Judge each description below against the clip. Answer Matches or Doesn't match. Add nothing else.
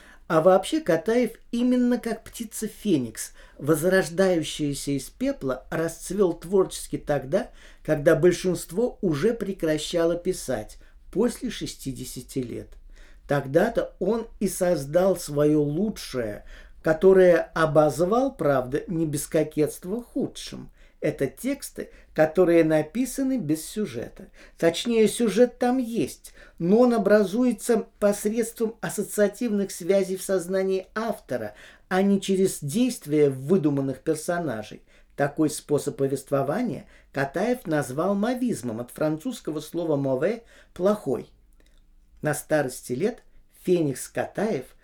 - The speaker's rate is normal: Doesn't match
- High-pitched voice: Doesn't match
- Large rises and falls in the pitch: Matches